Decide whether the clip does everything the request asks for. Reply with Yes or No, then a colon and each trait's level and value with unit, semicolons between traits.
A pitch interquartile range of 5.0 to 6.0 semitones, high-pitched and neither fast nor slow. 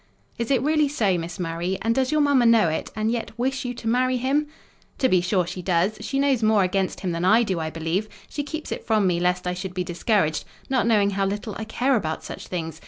No: wide, 5.6 semitones; high, 215 Hz; fast, 245 wpm